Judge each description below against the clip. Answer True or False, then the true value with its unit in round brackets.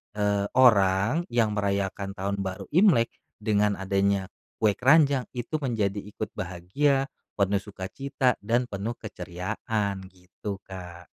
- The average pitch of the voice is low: True (100 Hz)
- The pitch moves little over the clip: False (3.6 semitones)